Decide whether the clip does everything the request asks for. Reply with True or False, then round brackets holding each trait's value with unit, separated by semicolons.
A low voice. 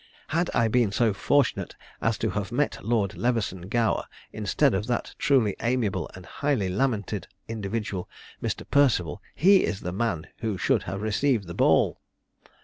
True (110 Hz)